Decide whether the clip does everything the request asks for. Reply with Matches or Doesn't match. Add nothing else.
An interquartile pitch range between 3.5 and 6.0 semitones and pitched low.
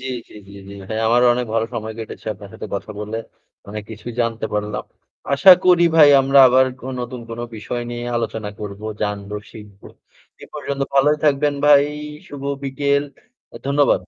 Matches